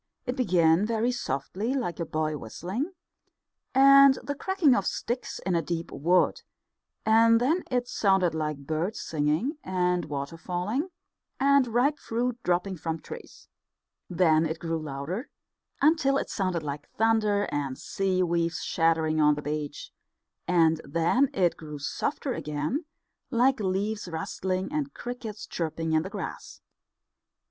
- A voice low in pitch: No, medium, 185 Hz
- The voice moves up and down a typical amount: No, wide, 7.2 semitones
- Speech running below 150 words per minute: Yes, average, 140 wpm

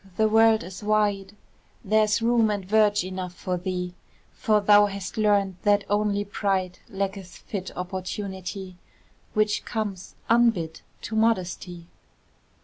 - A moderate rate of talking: No, slow, 125 wpm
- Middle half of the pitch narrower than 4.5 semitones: Yes, narrow, 2.4 semitones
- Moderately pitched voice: No, high, 200 Hz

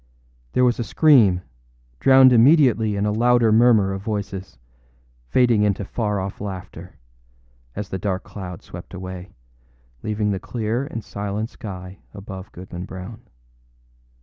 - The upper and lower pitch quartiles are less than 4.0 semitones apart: Yes, average, 3.4 semitones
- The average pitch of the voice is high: No, low, 105 Hz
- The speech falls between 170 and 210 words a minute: No, slow, 135 wpm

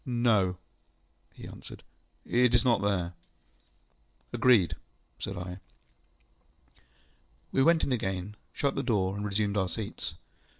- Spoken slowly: Yes, slow, 120 wpm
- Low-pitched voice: Yes, low, 100 Hz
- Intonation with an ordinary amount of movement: Yes, average, 4.6 semitones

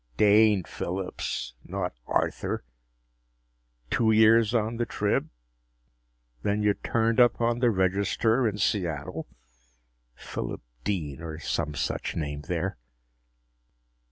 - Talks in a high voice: No, low, 100 Hz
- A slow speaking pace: Yes, slow, 105 wpm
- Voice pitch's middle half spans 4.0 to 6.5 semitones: Yes, average, 5.1 semitones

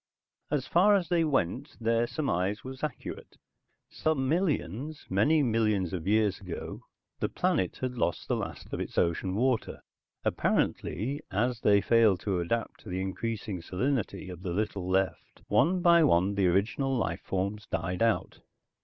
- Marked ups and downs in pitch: Yes, wide, 6.0 semitones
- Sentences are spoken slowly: No, average, 155 wpm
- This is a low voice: Yes, low, 110 Hz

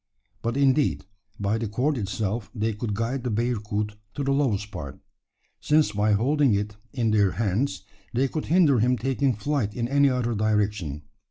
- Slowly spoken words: No, average, 170 wpm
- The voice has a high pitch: No, low, 115 Hz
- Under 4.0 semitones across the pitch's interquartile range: No, average, 4.3 semitones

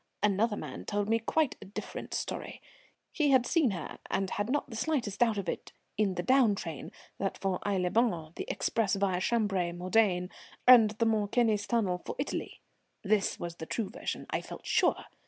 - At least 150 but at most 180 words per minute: No, average, 190 wpm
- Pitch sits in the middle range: No, high, 205 Hz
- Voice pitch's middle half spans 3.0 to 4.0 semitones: Yes, average, 3.5 semitones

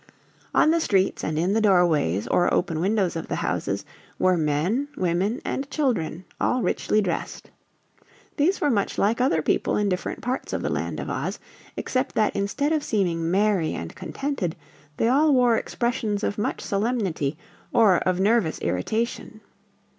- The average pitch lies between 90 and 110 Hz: No, high, 205 Hz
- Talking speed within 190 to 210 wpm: No, average, 160 wpm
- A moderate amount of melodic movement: No, wide, 5.8 semitones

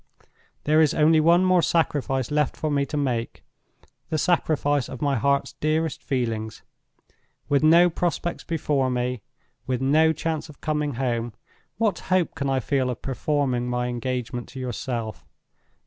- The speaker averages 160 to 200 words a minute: No, average, 145 wpm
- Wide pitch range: No, average, 3.9 semitones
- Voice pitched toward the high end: No, medium, 140 Hz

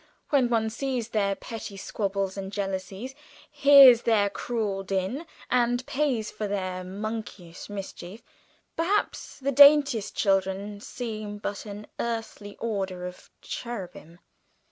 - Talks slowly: Yes, slow, 120 wpm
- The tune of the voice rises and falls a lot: No, average, 3.7 semitones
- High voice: Yes, high, 210 Hz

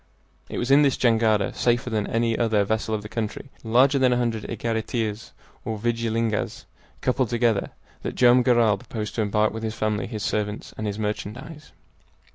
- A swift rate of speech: No, average, 175 wpm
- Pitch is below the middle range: Yes, low, 115 Hz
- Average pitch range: No, narrow, 2.0 semitones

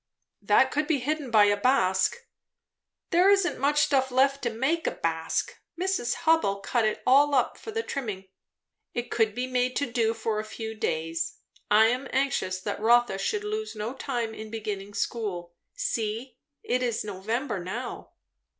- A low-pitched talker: No, high, 240 Hz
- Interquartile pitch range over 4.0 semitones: Yes, average, 4.6 semitones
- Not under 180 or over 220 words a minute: No, average, 170 wpm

